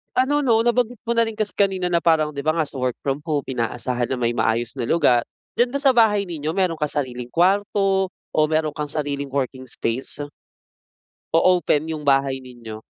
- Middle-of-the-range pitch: Yes, medium, 155 Hz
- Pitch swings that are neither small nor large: No, wide, 7.0 semitones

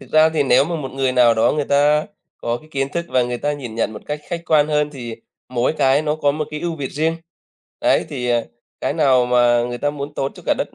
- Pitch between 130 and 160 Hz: Yes, medium, 140 Hz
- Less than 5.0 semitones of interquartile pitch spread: Yes, average, 3.5 semitones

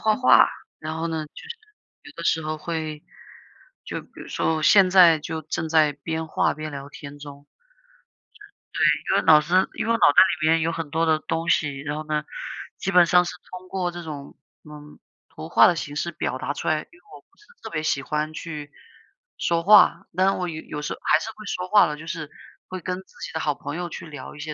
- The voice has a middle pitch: Yes, medium, 160 Hz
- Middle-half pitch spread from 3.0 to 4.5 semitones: No, narrow, 2.5 semitones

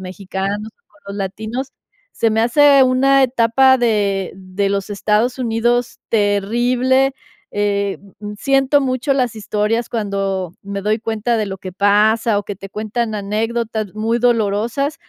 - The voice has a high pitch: Yes, high, 220 Hz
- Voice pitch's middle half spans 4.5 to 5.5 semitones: No, average, 3.2 semitones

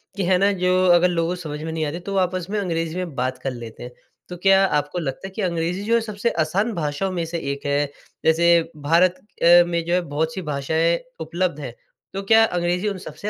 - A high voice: No, medium, 170 Hz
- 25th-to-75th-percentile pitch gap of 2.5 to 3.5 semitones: Yes, average, 2.9 semitones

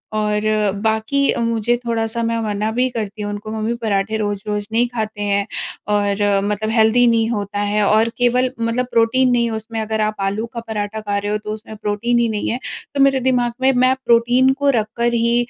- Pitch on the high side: Yes, high, 220 Hz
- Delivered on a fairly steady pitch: Yes, narrow, 2.2 semitones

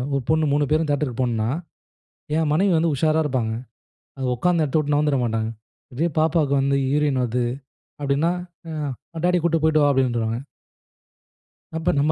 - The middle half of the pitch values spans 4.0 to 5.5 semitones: No, average, 3.6 semitones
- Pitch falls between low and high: Yes, medium, 145 Hz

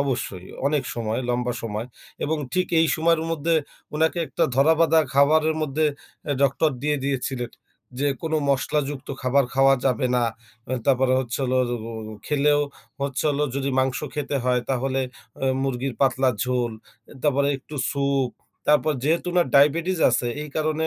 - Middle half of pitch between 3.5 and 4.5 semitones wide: No, average, 2.9 semitones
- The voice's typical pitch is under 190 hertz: Yes, medium, 140 Hz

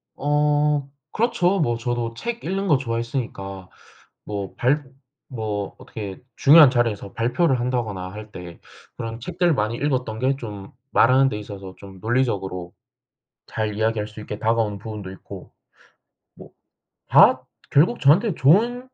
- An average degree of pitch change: No, wide, 5.7 semitones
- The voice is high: No, low, 115 Hz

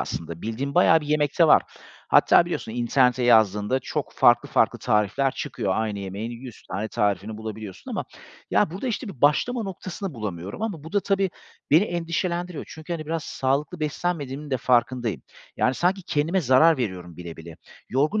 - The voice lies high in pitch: No, low, 135 Hz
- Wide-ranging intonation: Yes, wide, 7.3 semitones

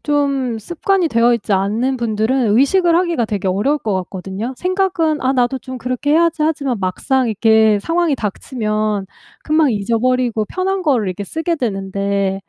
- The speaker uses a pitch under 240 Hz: No, high, 245 Hz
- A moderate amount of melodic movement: No, wide, 6.2 semitones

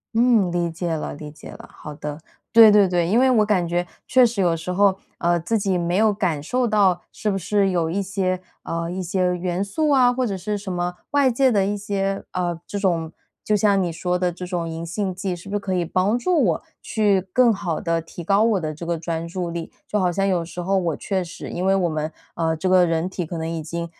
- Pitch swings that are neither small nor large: Yes, average, 3.1 semitones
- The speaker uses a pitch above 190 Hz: No, medium, 185 Hz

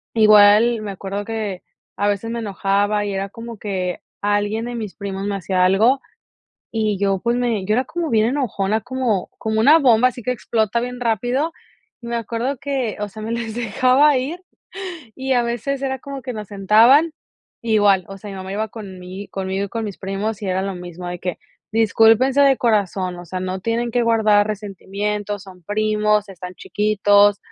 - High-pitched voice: Yes, high, 215 Hz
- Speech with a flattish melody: No, average, 3.1 semitones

